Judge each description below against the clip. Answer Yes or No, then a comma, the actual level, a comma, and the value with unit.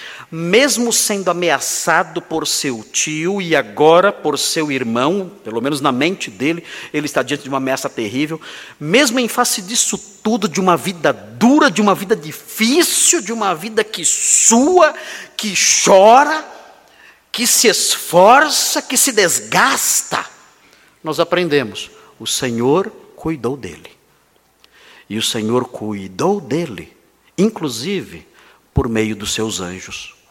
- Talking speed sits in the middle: Yes, average, 130 wpm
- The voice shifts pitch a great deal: Yes, wide, 8.0 semitones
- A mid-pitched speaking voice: Yes, medium, 175 Hz